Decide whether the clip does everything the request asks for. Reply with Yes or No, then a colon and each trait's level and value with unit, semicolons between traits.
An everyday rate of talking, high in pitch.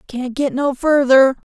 Yes: average, 160 wpm; very high, 265 Hz